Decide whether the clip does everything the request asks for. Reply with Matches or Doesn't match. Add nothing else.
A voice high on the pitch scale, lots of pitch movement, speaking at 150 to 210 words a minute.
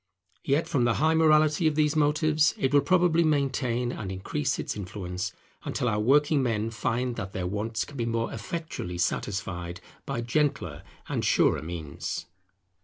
Doesn't match